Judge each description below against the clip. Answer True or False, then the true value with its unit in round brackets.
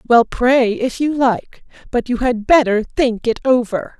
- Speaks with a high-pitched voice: True (240 Hz)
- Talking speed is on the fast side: False (180 wpm)